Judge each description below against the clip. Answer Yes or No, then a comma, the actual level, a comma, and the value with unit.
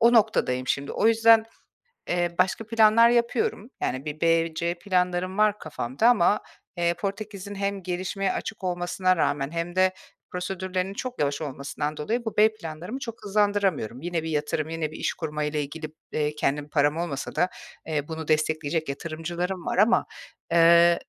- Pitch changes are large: No, average, 4.5 semitones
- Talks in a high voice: No, medium, 175 Hz